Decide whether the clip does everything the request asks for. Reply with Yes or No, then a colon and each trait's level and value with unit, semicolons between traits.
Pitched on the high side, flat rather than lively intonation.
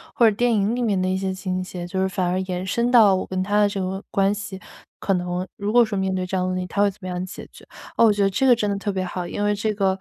Yes: high, 195 Hz; narrow, 1.9 semitones